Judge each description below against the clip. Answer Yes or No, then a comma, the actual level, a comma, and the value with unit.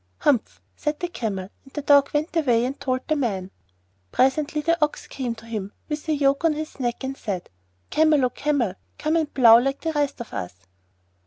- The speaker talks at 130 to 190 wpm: No, average, 200 wpm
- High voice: Yes, very high, 275 Hz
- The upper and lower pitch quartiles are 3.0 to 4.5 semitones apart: Yes, average, 4.2 semitones